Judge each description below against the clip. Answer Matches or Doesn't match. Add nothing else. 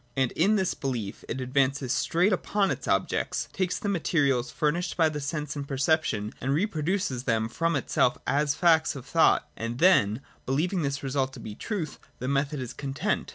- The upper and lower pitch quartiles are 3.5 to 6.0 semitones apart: Matches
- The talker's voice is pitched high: Doesn't match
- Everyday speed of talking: Matches